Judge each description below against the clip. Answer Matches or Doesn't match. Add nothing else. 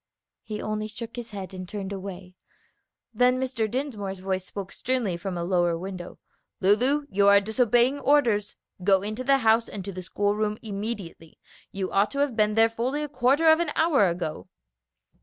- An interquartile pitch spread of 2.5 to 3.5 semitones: Doesn't match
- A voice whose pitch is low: Doesn't match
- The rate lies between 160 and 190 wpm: Matches